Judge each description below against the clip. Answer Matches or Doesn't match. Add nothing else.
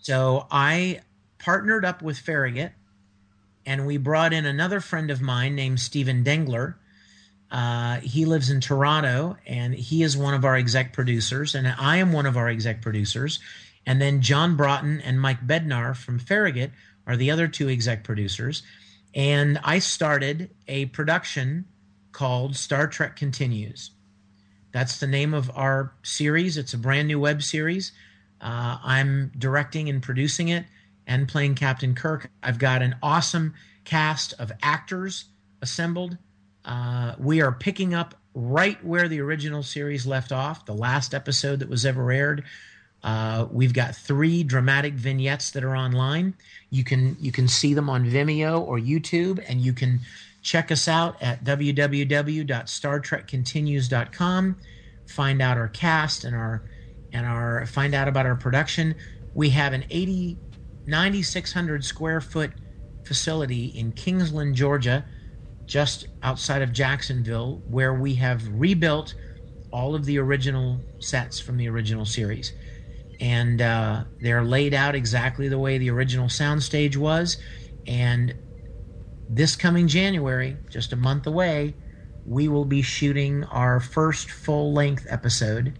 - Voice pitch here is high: Doesn't match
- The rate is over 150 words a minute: Doesn't match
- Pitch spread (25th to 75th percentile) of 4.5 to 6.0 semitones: Doesn't match